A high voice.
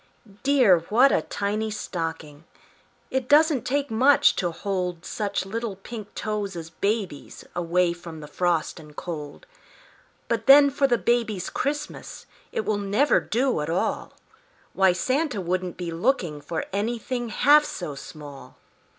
Yes: high, 200 Hz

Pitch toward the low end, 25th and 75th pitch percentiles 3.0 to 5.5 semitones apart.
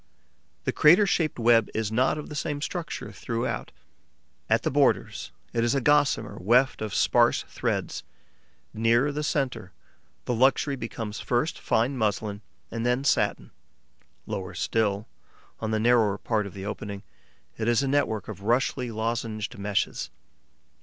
Yes: low, 115 Hz; average, 3.8 semitones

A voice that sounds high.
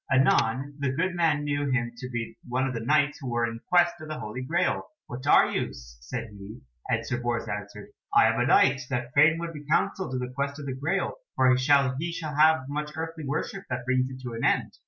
No: low, 130 Hz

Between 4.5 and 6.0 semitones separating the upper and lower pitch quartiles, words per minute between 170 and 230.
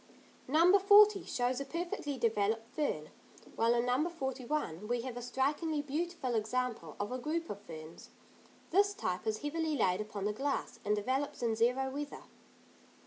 No: wide, 5.6 semitones; average, 160 wpm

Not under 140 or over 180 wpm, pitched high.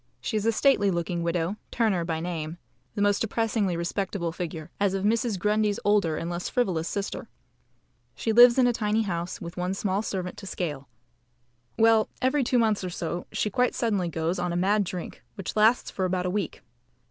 No: average, 195 wpm; high, 195 Hz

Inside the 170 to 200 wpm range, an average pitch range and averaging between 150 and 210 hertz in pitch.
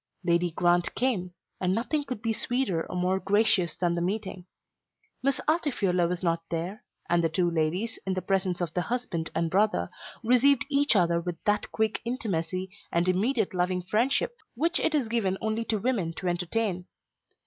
Yes: average, 175 wpm; average, 4.6 semitones; high, 190 Hz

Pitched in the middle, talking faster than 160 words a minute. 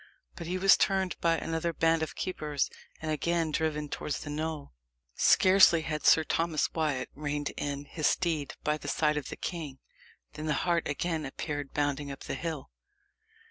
Yes: medium, 155 Hz; average, 175 wpm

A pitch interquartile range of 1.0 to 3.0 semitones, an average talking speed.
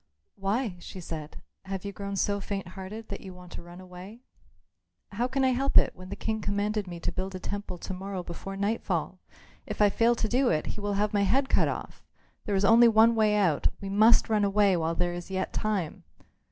No: narrow, 2.6 semitones; fast, 220 wpm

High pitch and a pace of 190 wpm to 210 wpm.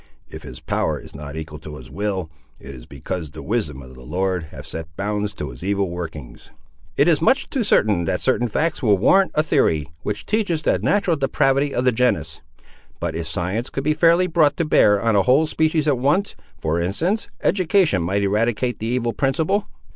No: low, 110 Hz; average, 200 wpm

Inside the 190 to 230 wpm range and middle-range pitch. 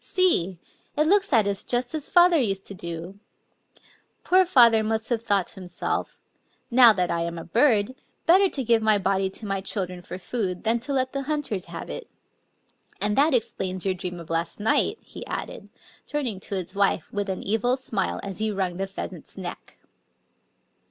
No: average, 195 wpm; high, 210 Hz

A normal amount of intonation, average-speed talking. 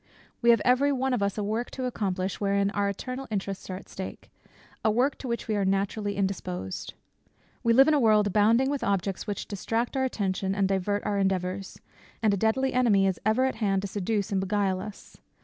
No: average, 3.3 semitones; fast, 210 wpm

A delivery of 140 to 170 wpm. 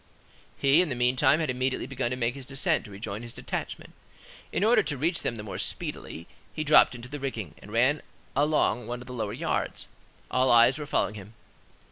No: fast, 205 wpm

